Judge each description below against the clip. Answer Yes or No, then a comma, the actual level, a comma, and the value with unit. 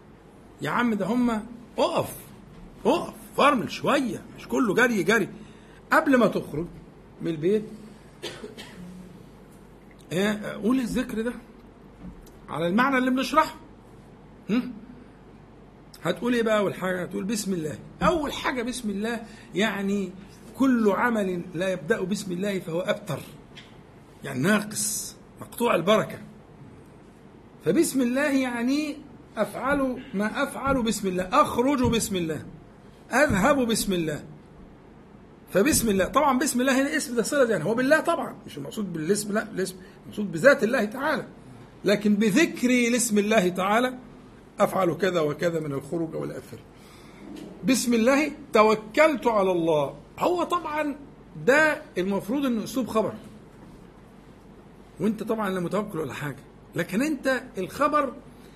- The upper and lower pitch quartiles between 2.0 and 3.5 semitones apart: No, average, 5.3 semitones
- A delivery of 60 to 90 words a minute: No, average, 120 wpm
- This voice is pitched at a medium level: No, high, 220 Hz